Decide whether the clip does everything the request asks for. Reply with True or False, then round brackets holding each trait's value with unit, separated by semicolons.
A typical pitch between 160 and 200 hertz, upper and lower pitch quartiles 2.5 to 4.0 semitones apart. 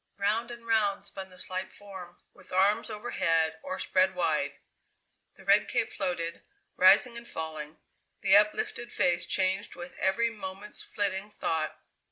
True (190 Hz; 2.9 semitones)